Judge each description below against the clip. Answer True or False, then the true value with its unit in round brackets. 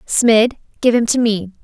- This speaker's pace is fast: False (185 wpm)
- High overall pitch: True (225 Hz)